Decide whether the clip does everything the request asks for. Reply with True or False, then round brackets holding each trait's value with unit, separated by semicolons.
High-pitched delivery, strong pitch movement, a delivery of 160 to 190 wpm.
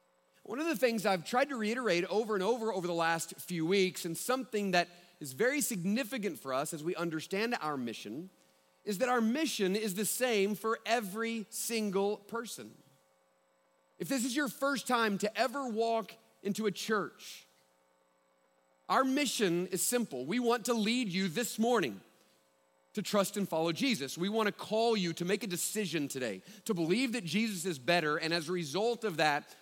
True (200 Hz; 5.7 semitones; 180 wpm)